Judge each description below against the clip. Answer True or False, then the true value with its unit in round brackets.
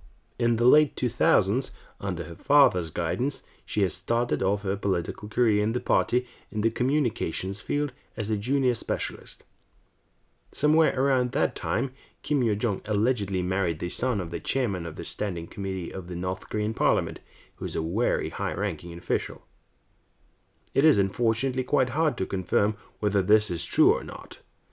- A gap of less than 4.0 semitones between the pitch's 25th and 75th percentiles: False (4.5 semitones)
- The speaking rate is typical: True (165 wpm)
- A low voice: True (105 Hz)